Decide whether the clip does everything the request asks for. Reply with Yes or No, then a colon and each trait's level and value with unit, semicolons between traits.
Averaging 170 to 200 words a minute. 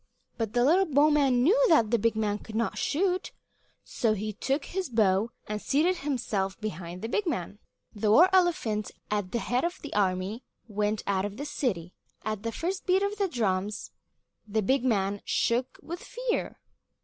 Yes: average, 185 wpm